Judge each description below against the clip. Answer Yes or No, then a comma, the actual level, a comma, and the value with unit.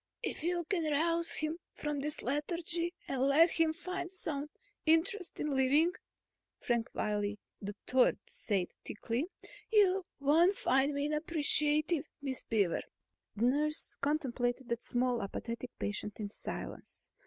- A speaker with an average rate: No, slow, 130 wpm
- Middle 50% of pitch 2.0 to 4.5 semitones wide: No, average, 5.2 semitones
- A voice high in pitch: Yes, very high, 295 Hz